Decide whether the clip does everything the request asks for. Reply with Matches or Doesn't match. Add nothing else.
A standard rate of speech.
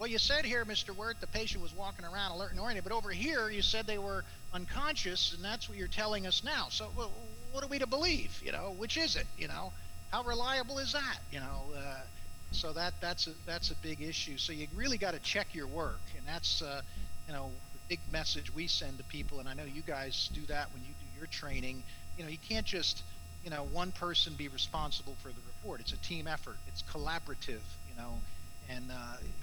Doesn't match